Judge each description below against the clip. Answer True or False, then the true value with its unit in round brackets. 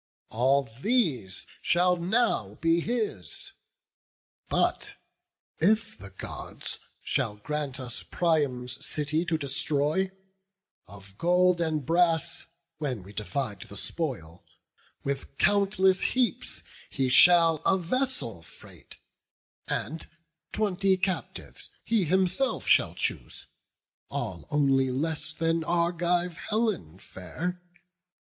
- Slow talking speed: True (100 wpm)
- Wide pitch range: True (5.7 semitones)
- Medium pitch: True (160 Hz)